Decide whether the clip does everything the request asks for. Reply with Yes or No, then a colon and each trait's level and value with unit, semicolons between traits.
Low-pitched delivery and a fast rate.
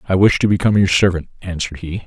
Yes: very low, 95 Hz; fast, 230 wpm